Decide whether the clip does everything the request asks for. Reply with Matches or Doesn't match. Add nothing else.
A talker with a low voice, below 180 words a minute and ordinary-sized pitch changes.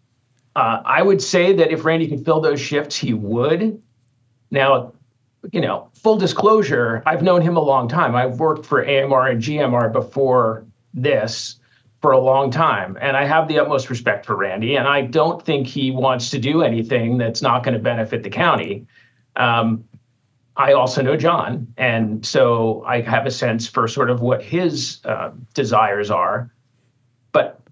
Matches